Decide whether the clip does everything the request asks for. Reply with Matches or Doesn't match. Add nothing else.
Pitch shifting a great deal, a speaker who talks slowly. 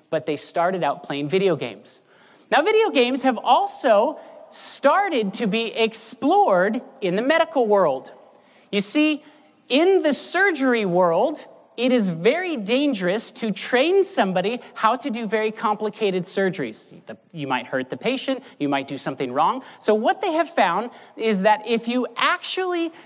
Doesn't match